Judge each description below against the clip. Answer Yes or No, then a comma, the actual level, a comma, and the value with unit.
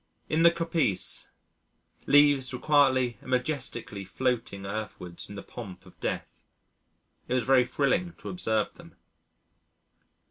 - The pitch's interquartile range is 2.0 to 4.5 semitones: No, average, 5.1 semitones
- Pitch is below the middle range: Yes, low, 130 Hz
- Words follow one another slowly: Yes, slow, 130 wpm